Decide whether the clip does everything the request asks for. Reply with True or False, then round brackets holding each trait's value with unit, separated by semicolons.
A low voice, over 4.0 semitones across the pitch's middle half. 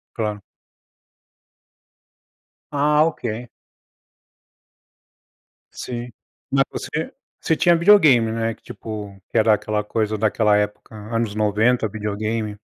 False (110 Hz; 2.6 semitones)